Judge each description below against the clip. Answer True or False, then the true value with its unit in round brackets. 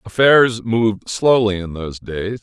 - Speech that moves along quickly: False (150 wpm)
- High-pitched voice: False (105 Hz)